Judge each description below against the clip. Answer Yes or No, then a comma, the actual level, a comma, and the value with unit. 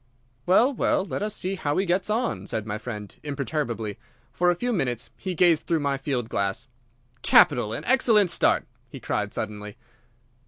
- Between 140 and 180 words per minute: Yes, average, 170 wpm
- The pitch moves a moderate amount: No, wide, 8.8 semitones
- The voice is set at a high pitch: No, medium, 150 Hz